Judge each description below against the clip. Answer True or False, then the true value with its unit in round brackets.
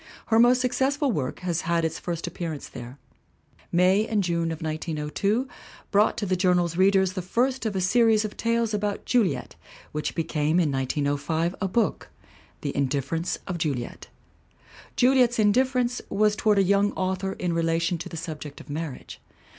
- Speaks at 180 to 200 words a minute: False (160 wpm)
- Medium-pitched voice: True (180 Hz)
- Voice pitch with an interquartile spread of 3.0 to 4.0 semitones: False (4.9 semitones)